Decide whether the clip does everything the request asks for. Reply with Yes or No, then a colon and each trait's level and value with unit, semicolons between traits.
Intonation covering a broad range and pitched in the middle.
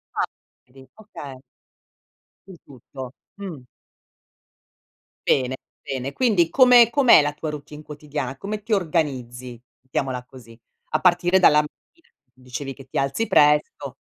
Yes: wide, 5.7 semitones; medium, 145 Hz